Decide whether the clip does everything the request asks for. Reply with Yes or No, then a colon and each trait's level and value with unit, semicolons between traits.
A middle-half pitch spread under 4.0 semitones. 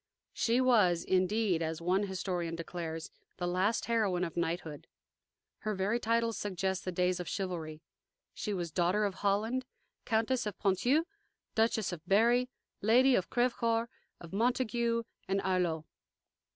No: average, 4.5 semitones